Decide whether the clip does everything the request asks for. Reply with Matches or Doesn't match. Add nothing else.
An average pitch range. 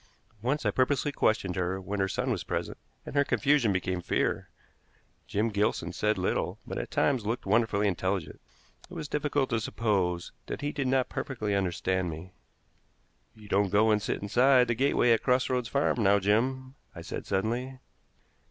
Matches